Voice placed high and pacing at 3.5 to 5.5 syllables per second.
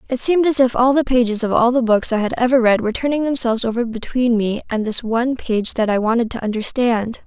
No: high, 240 Hz; 6.1 syllables/s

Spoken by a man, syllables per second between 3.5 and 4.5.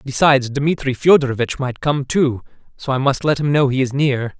No: male; 5.3 syllables/s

